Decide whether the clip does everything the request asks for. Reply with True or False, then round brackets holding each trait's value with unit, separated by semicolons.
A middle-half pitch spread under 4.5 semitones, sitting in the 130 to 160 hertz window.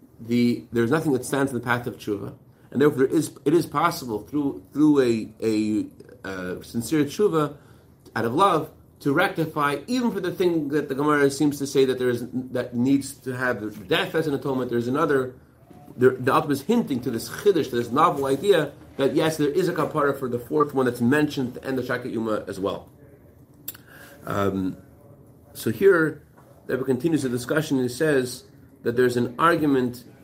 True (3.6 semitones; 135 Hz)